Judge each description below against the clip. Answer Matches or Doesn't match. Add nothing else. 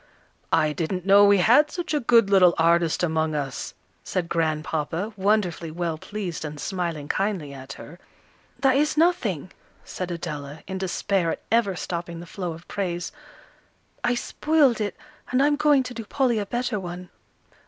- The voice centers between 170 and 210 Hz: Matches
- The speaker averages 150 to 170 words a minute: Matches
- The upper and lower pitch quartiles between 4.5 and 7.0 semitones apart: Matches